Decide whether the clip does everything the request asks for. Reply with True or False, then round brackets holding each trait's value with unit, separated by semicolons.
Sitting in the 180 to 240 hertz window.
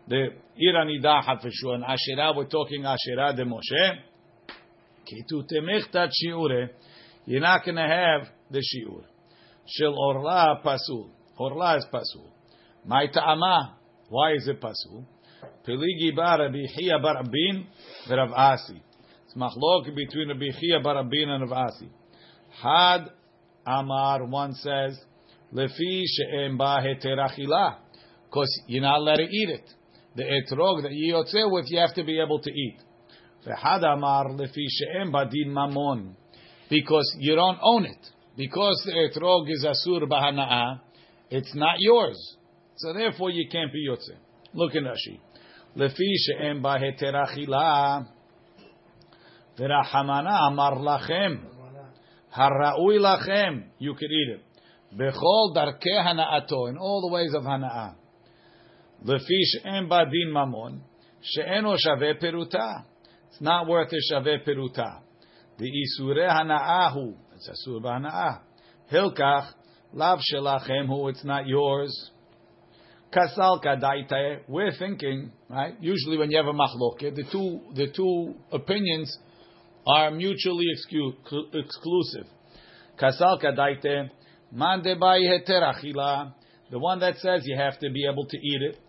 False (145 Hz)